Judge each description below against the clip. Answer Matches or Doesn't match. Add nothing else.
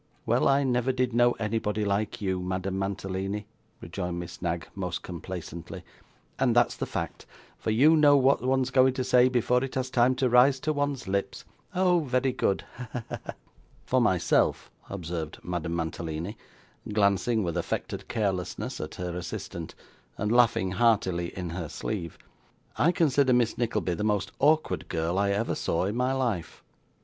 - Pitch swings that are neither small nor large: Doesn't match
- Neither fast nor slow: Matches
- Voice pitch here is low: Matches